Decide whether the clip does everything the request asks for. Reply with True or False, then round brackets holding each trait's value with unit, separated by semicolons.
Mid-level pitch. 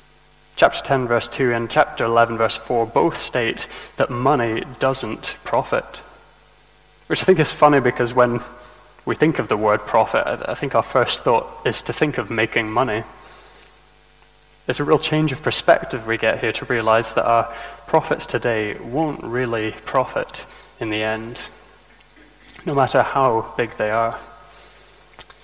False (125 Hz)